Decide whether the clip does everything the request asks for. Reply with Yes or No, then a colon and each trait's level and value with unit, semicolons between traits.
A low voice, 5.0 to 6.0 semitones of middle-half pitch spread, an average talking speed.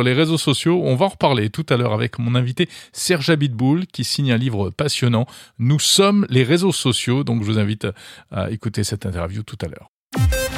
Yes: low, 125 Hz; wide, 5.6 semitones; average, 205 wpm